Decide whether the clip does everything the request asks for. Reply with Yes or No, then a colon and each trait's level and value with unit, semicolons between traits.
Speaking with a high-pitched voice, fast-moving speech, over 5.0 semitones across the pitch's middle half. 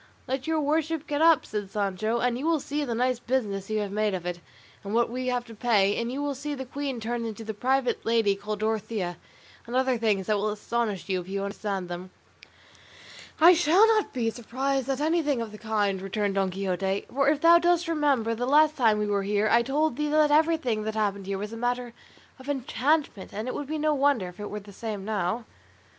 Yes: high, 235 Hz; fast, 225 wpm; wide, 5.5 semitones